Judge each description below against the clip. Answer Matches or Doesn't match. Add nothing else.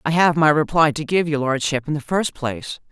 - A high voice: Doesn't match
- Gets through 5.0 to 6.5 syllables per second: Matches